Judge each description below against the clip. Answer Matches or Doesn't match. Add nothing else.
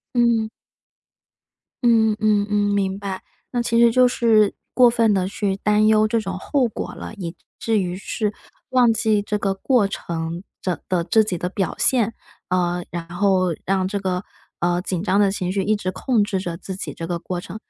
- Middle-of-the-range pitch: Doesn't match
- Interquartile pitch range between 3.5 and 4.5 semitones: Doesn't match